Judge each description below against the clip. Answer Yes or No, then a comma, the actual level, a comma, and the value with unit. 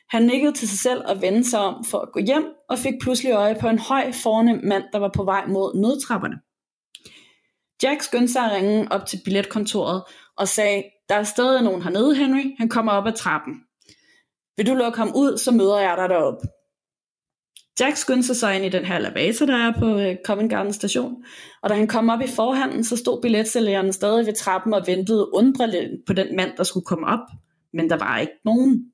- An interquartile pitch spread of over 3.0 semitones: Yes, average, 4.2 semitones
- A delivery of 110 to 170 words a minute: No, average, 210 wpm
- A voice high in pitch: Yes, high, 220 Hz